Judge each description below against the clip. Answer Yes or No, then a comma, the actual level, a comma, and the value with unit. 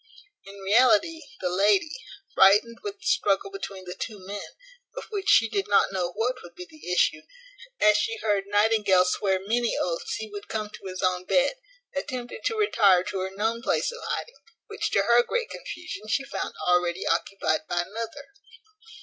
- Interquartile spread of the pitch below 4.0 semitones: No, average, 4.9 semitones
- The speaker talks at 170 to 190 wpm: Yes, average, 180 wpm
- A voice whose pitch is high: Yes, high, 210 Hz